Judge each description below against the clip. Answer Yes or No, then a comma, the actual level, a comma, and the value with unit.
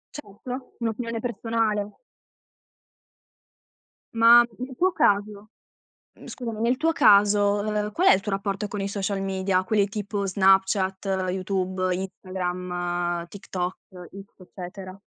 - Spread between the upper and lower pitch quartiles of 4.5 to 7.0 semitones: No, narrow, 2.4 semitones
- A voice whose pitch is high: Yes, high, 200 Hz